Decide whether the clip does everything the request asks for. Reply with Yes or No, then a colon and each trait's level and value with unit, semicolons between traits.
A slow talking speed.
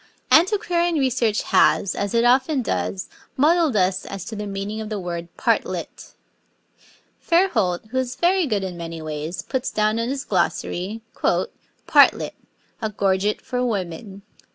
No: average, 145 wpm